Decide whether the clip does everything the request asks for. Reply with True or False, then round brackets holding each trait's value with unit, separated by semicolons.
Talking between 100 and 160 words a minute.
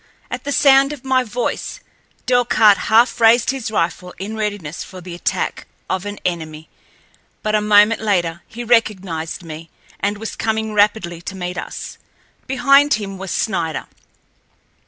True (150 wpm)